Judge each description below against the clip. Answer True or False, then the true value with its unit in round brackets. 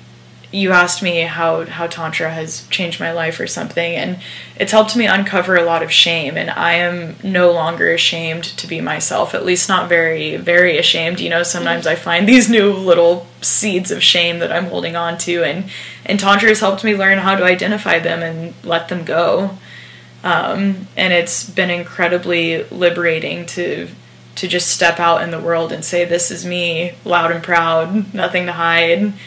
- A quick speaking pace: False (190 wpm)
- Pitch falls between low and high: True (175 Hz)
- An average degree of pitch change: False (1.8 semitones)